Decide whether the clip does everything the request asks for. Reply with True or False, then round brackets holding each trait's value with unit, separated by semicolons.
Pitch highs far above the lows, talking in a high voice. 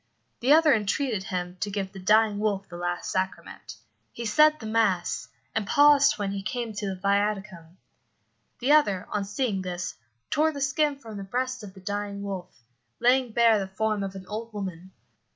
False (3.9 semitones; 205 Hz)